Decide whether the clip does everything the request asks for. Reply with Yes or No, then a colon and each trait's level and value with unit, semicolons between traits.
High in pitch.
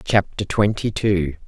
No: low, 100 Hz